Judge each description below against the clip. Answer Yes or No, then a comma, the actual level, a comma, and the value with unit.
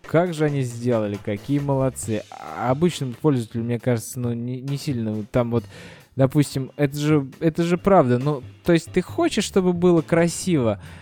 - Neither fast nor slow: No, fast, 175 wpm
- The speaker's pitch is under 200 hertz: Yes, low, 135 Hz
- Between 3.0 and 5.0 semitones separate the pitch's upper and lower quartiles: No, wide, 5.6 semitones